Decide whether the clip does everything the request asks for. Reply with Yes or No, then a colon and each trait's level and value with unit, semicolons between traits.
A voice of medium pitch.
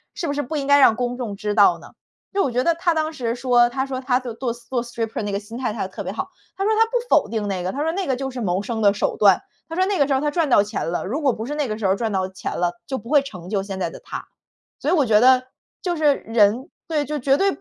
No: very high, 250 Hz